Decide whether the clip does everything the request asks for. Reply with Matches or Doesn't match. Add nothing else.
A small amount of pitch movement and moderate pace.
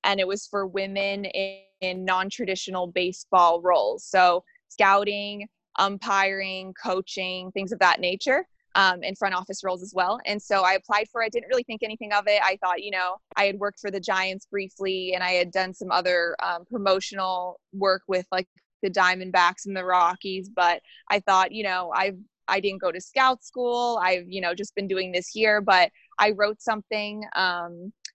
Matches